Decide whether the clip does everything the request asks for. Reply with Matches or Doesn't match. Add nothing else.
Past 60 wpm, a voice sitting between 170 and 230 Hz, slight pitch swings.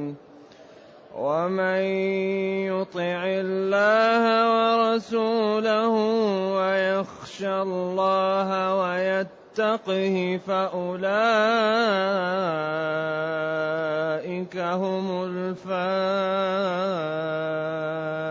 Doesn't match